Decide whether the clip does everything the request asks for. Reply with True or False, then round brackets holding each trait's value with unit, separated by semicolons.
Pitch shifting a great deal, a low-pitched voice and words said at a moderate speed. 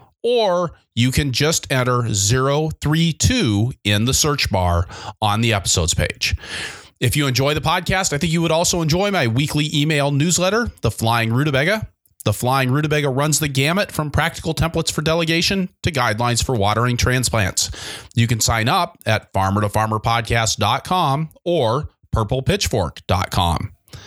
True (5.7 semitones; 130 Hz; 145 wpm)